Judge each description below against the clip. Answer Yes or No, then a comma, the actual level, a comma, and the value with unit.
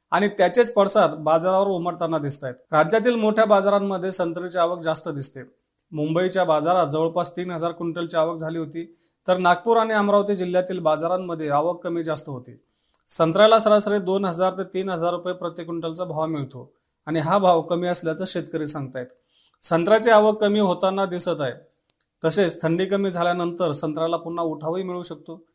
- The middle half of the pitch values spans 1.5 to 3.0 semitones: Yes, narrow, 2.6 semitones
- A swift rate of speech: Yes, fast, 155 wpm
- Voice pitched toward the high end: No, medium, 175 Hz